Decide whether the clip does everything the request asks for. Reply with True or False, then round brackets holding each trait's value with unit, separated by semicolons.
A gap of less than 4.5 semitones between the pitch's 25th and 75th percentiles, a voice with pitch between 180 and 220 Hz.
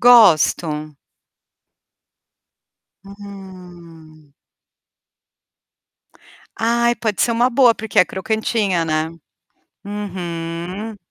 False (4.9 semitones; 190 Hz)